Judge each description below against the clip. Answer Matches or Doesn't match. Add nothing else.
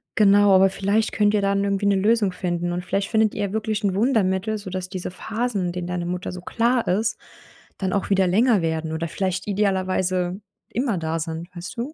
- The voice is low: Doesn't match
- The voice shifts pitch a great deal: Doesn't match